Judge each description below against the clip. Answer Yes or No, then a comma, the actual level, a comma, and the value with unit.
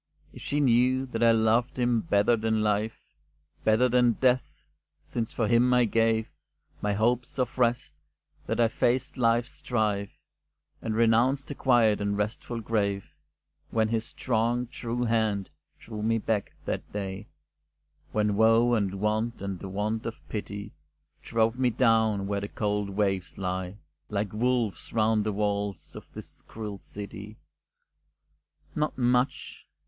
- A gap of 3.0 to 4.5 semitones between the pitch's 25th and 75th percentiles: No, narrow, 2.6 semitones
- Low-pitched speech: Yes, low, 110 Hz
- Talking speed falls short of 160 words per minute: Yes, average, 145 wpm